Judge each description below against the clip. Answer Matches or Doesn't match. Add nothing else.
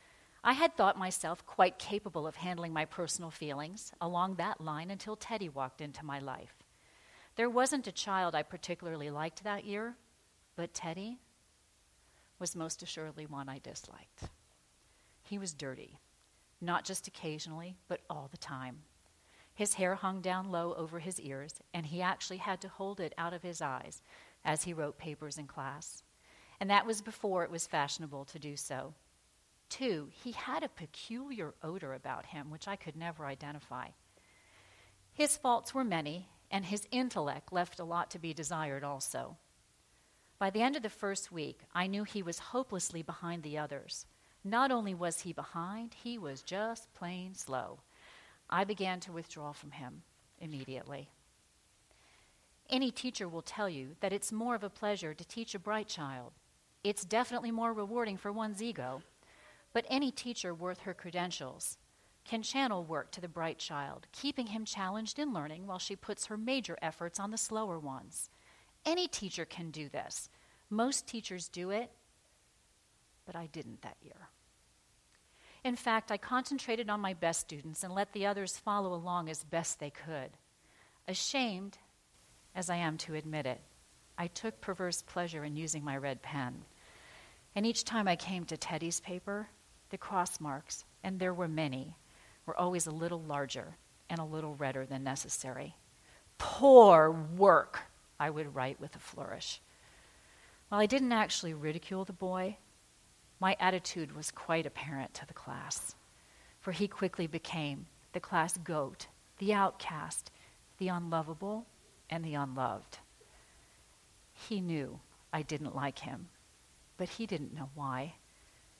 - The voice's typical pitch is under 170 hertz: Doesn't match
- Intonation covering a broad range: Doesn't match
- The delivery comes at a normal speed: Matches